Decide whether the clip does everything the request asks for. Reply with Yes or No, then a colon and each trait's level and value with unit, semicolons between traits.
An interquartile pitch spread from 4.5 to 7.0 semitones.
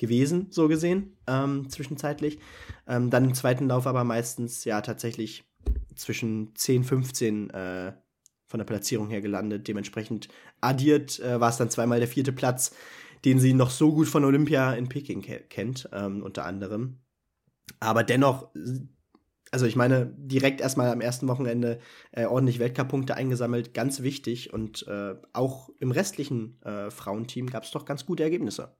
No: average, 3.3 semitones